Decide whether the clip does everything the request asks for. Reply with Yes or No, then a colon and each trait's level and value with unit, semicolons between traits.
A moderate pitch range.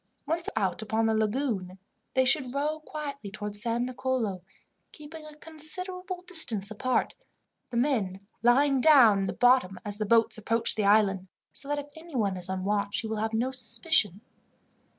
No: wide, 5.9 semitones